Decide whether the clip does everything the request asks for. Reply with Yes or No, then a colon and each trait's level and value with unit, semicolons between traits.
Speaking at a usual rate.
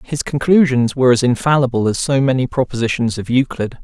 Yes: average, 170 wpm